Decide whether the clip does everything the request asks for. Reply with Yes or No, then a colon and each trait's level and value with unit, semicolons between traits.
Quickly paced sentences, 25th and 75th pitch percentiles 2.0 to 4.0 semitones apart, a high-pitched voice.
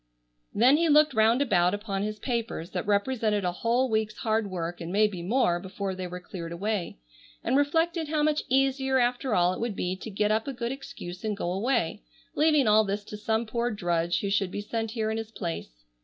No: fast, 215 wpm; average, 4.6 semitones; high, 215 Hz